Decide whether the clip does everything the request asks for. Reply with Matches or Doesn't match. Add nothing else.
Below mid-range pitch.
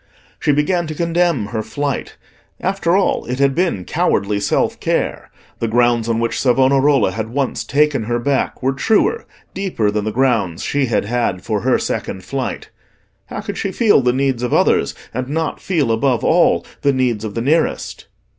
Matches